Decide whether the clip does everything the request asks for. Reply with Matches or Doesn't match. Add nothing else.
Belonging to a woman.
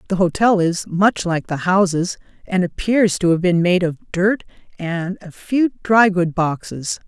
Matches